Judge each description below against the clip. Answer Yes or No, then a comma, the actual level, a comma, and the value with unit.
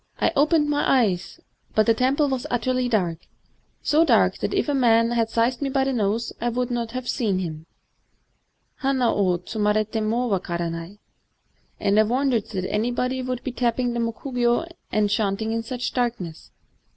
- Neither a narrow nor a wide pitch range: Yes, average, 3.4 semitones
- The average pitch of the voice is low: No, high, 235 Hz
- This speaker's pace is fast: No, average, 175 wpm